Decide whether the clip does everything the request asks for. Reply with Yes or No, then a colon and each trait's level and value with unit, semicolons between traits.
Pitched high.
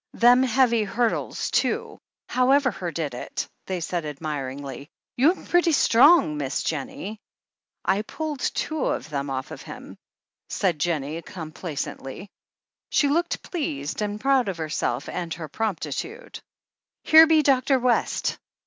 Yes: high, 195 Hz